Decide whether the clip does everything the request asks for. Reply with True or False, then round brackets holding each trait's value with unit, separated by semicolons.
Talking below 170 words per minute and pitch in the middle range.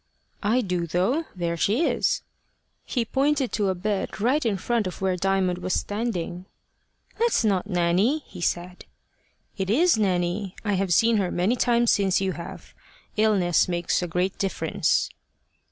False (155 wpm; 195 Hz)